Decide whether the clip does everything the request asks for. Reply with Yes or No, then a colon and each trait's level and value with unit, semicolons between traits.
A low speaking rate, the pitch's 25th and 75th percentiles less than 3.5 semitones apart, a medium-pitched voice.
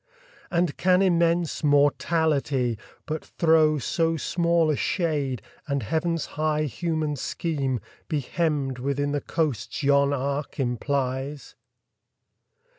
Yes: slow, 110 wpm; average, 2.8 semitones; medium, 150 Hz